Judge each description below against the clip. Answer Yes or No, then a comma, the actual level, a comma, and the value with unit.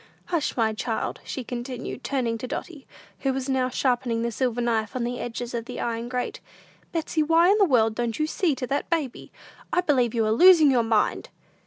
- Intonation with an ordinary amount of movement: Yes, average, 3.6 semitones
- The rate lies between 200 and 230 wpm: Yes, fast, 205 wpm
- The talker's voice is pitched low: No, very high, 250 Hz